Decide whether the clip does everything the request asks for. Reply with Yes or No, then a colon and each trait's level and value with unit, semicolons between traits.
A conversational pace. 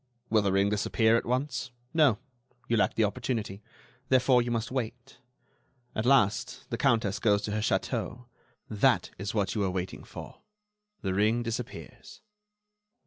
Yes: average, 150 wpm